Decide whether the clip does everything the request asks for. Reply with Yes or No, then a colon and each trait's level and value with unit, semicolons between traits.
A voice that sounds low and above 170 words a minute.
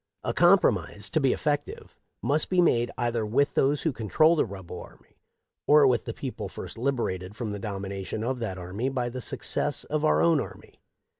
Yes: low, 120 Hz; average, 190 wpm